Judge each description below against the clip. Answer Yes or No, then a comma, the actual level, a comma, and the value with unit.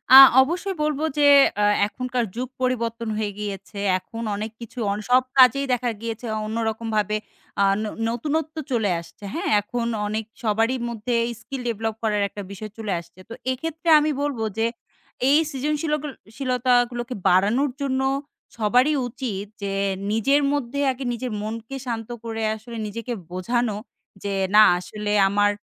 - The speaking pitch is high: Yes, high, 235 Hz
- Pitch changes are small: No, average, 3.4 semitones